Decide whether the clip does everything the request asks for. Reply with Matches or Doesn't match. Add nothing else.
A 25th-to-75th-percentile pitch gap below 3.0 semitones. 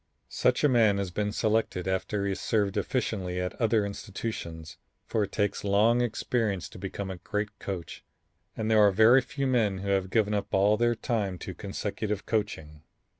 Matches